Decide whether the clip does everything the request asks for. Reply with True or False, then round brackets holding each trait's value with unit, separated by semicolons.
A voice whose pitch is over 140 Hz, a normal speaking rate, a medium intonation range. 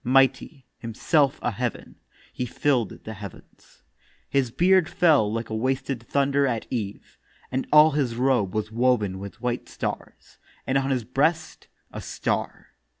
False (125 Hz; 150 wpm; 3.5 semitones)